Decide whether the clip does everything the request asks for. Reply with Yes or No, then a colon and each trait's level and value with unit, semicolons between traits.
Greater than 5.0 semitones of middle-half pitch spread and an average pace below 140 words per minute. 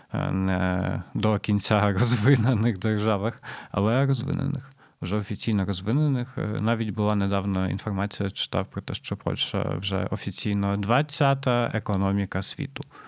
No: average, 3.5 semitones; average, 110 wpm